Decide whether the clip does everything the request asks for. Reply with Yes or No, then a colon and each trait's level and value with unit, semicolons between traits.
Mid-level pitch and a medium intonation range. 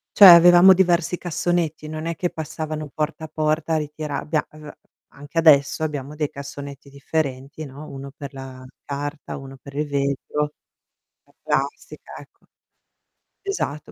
No: medium, 150 Hz; narrow, 2.3 semitones